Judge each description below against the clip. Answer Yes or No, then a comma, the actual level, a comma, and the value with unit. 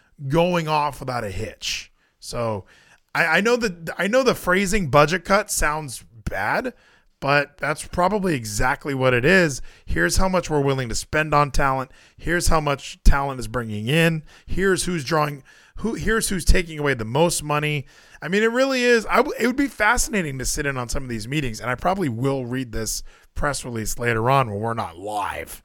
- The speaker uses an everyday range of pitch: No, wide, 5.8 semitones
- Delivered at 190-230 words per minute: Yes, average, 200 wpm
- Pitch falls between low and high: Yes, medium, 150 Hz